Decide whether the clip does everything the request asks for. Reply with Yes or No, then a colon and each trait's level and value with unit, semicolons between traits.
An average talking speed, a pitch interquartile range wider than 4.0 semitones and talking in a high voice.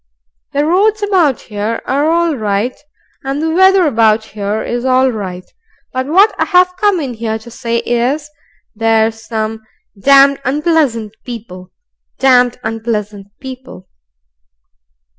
No: slow, 125 wpm; wide, 5.4 semitones; very high, 250 Hz